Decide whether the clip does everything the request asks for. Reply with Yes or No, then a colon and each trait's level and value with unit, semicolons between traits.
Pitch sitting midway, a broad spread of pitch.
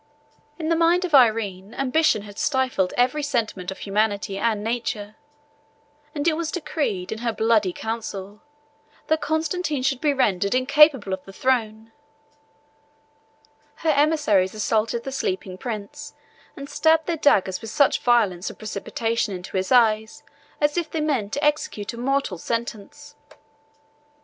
No: high, 235 Hz; wide, 6.2 semitones